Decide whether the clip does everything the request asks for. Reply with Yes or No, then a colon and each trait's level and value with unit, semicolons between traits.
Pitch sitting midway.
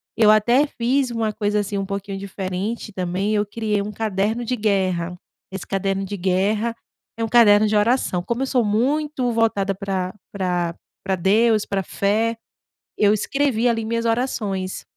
No: high, 210 Hz